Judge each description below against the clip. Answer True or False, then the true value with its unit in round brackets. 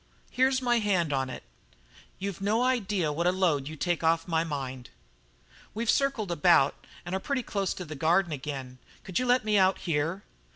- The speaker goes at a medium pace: True (190 wpm)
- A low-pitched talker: False (175 Hz)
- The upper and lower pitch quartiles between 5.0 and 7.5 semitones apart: True (5.3 semitones)